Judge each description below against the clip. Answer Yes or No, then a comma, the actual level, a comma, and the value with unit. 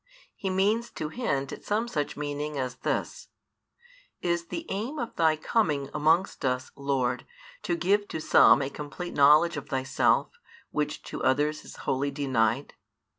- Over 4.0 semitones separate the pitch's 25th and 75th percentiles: Yes, average, 5.3 semitones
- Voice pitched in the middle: Yes, medium, 150 Hz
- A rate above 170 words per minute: No, average, 155 wpm